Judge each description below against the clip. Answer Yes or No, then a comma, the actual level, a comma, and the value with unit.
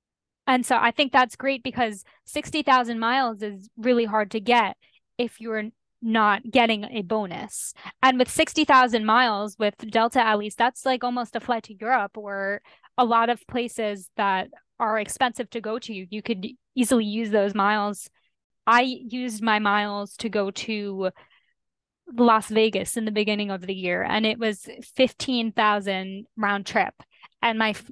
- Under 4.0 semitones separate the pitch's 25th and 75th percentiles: Yes, average, 2.8 semitones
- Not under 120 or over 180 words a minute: Yes, average, 160 wpm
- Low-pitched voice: No, high, 225 Hz